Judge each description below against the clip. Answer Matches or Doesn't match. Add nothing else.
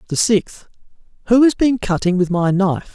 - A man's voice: Matches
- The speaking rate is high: Doesn't match